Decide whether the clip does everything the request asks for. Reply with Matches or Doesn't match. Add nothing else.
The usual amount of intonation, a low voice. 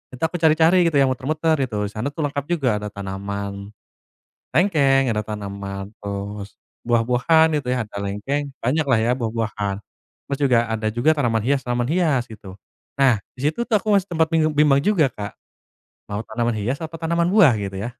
Doesn't match